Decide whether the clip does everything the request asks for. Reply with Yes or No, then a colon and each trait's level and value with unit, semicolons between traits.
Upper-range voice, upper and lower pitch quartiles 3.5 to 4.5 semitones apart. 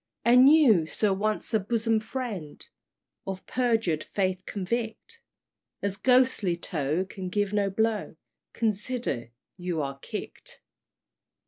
Yes: high, 205 Hz; average, 4.1 semitones